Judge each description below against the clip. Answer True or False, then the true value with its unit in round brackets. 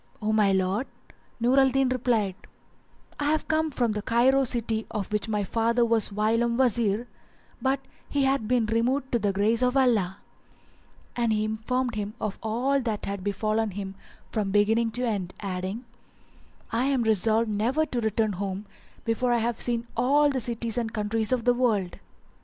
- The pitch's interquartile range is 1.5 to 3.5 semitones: True (2.9 semitones)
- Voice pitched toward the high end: True (225 Hz)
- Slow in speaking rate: False (170 wpm)